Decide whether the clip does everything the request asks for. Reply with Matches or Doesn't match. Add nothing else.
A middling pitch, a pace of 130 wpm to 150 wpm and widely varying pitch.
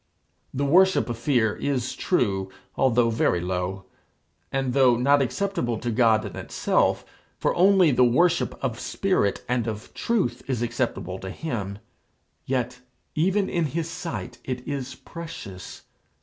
Doesn't match